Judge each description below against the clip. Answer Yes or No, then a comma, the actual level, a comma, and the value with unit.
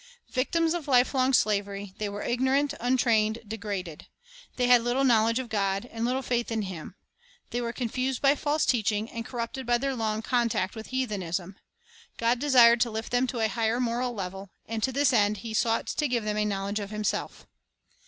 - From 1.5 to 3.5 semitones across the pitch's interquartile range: Yes, average, 3.1 semitones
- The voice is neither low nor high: No, high, 230 Hz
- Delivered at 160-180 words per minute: No, average, 195 wpm